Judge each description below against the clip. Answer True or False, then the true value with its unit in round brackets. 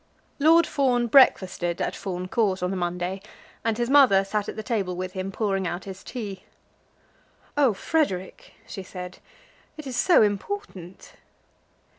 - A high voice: True (195 Hz)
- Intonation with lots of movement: False (4.9 semitones)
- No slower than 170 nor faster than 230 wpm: False (150 wpm)